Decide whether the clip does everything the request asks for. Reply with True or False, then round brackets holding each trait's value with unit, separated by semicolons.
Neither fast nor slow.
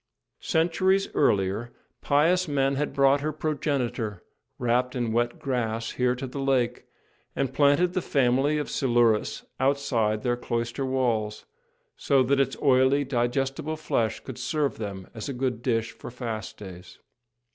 True (145 wpm)